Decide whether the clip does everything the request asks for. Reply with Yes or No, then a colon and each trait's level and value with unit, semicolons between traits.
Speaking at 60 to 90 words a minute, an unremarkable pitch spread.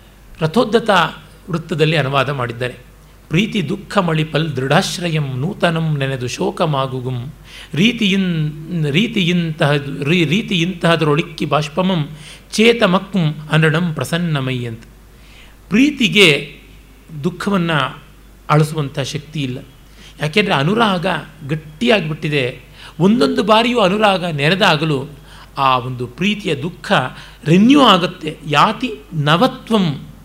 Yes: average, 80 wpm; average, 4.8 semitones